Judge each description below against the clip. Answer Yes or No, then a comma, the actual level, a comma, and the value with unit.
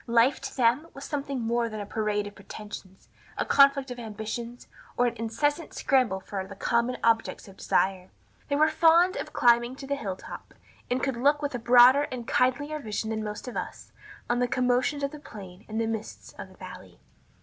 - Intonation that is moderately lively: Yes, average, 4.1 semitones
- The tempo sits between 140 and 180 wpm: No, fast, 205 wpm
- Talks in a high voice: Yes, high, 240 Hz